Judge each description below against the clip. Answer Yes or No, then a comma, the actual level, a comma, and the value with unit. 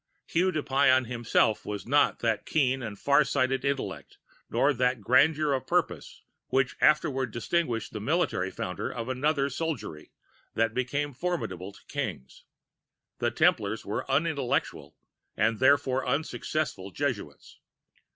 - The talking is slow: Yes, slow, 130 wpm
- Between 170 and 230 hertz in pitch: No, low, 130 Hz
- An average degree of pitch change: Yes, average, 4.3 semitones